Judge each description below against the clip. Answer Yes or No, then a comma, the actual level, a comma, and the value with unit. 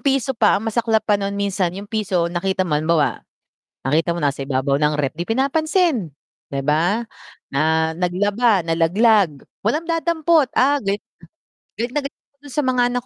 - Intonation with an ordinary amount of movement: No, wide, 7.2 semitones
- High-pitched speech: Yes, high, 200 Hz